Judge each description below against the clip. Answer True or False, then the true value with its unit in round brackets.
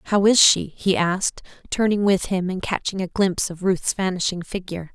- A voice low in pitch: False (190 Hz)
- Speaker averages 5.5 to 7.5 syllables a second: False (5.2 syllables/s)